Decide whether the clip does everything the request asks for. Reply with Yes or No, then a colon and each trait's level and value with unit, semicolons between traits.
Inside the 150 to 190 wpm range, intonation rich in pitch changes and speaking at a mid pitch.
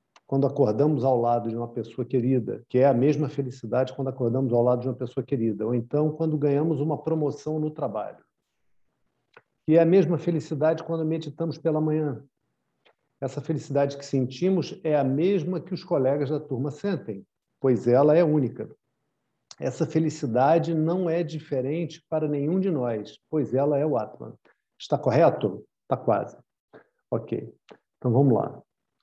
No: average, 160 wpm; average, 3.5 semitones; medium, 145 Hz